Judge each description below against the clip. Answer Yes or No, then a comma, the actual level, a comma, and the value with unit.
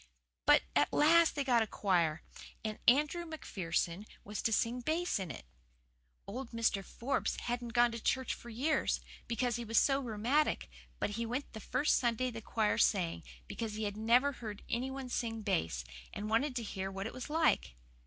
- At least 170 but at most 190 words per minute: Yes, average, 185 wpm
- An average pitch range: Yes, average, 3.9 semitones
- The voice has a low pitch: No, high, 230 Hz